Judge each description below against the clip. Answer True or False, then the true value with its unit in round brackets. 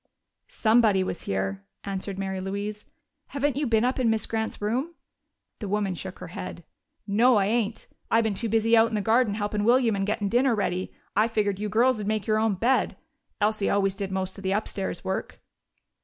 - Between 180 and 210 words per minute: True (195 wpm)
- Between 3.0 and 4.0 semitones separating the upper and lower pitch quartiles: False (2.6 semitones)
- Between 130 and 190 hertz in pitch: False (210 Hz)